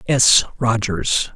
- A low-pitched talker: Yes, low, 115 Hz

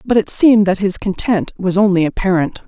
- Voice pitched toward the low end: No, high, 200 Hz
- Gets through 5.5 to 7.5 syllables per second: Yes, 5.6 syllables/s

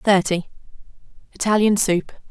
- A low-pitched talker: No, high, 195 Hz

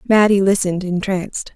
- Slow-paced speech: Yes, slow, 115 wpm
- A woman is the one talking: Yes, female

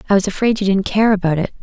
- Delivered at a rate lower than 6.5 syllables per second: No, 7.3 syllables/s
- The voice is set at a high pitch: Yes, high, 195 Hz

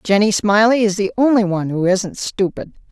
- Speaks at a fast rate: No, average, 185 wpm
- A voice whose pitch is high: Yes, high, 205 Hz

